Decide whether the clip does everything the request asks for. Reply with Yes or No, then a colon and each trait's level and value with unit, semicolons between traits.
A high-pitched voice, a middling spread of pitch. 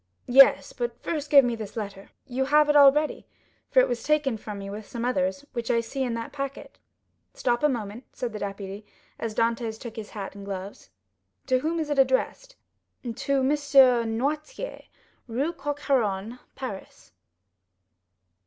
Yes: very high, 250 Hz; average, 4.3 semitones